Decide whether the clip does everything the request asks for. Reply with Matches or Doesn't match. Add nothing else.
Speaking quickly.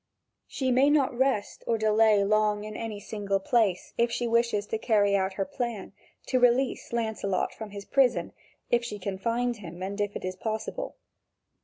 Doesn't match